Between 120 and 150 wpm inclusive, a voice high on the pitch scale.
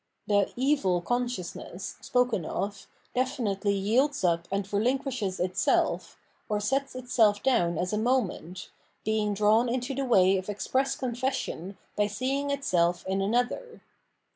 Yes: average, 140 wpm; high, 215 Hz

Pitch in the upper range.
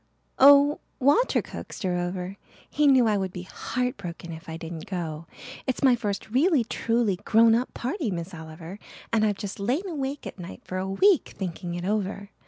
Yes: high, 205 Hz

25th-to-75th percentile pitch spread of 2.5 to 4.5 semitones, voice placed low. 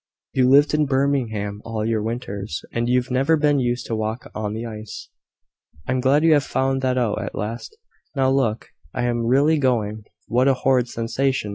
Yes: average, 3.1 semitones; low, 125 Hz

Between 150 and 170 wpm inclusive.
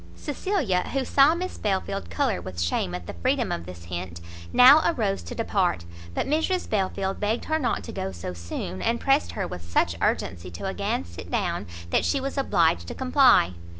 No: average, 190 wpm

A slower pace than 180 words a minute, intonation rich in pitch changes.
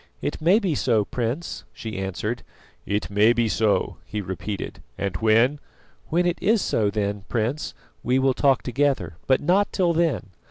Yes: average, 170 wpm; wide, 6.1 semitones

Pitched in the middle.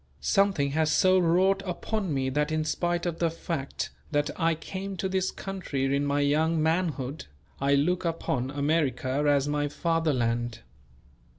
Yes: medium, 155 Hz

